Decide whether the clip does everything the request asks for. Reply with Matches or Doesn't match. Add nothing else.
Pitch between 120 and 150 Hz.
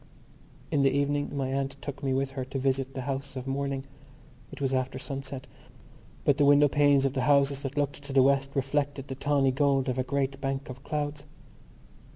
Matches